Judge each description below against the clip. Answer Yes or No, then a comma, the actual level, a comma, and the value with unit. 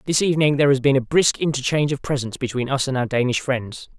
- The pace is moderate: No, fast, 240 wpm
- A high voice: No, low, 135 Hz